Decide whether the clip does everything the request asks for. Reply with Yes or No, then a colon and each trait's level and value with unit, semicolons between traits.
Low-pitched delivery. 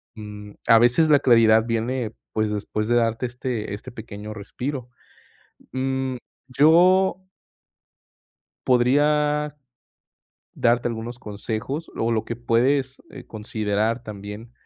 Yes: low, 120 Hz